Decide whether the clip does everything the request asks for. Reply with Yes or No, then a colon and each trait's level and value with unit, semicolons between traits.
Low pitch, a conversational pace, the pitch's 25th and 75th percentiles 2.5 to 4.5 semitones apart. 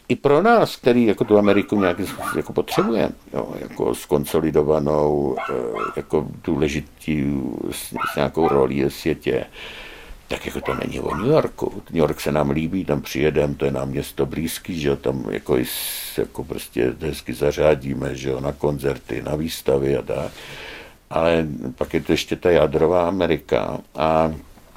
Yes: very low, 75 Hz; average, 155 wpm; average, 2.8 semitones